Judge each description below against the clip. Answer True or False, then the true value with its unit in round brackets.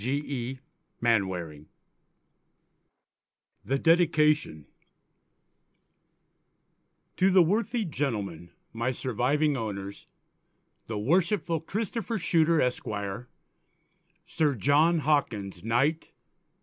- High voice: False (140 Hz)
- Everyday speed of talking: False (75 wpm)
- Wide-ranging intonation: True (7.1 semitones)